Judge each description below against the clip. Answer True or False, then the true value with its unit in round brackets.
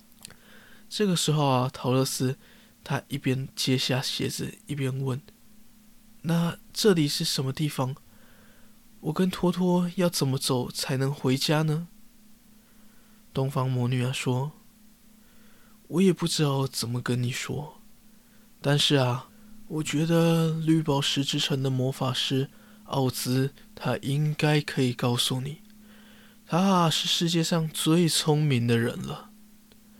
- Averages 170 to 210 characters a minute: True (180 characters per minute)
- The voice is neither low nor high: True (155 Hz)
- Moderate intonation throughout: False (8.2 semitones)